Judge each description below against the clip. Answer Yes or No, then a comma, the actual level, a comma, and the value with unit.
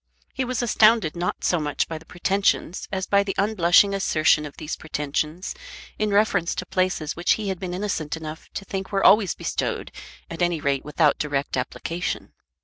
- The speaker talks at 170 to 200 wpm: Yes, average, 180 wpm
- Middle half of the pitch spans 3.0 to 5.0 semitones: Yes, average, 4.2 semitones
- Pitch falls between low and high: Yes, medium, 175 Hz